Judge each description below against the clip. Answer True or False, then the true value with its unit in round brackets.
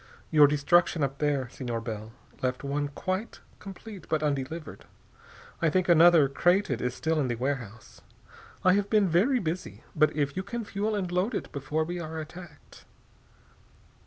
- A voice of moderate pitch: True (155 Hz)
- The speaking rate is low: False (160 wpm)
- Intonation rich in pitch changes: False (4.8 semitones)